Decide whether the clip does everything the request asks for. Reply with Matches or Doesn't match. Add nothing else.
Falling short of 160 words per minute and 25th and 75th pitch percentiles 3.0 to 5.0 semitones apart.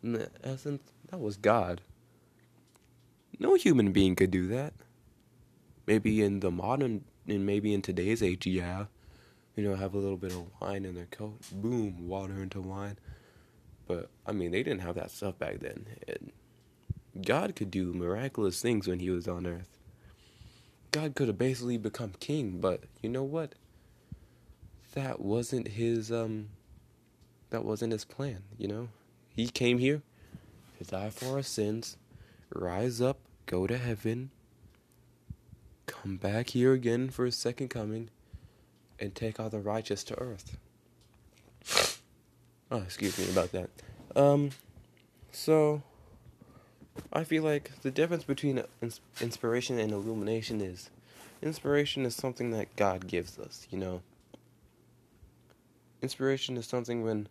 Matches